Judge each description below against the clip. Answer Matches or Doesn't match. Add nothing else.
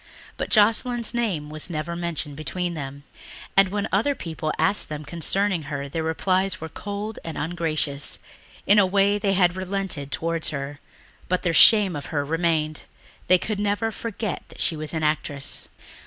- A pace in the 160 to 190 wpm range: Matches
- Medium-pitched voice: Matches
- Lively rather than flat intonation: Doesn't match